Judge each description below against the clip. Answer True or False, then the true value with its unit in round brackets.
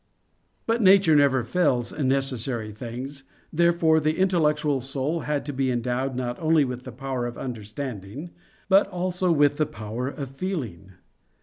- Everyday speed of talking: True (150 wpm)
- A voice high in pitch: False (135 Hz)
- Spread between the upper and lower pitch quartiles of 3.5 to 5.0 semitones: True (4.4 semitones)